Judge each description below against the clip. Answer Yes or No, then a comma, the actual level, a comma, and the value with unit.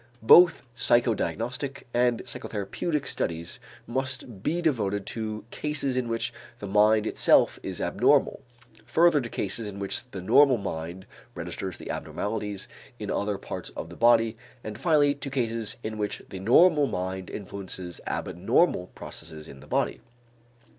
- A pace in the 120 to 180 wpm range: Yes, average, 140 wpm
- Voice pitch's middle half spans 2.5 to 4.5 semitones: No, average, 5.1 semitones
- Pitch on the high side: No, low, 110 Hz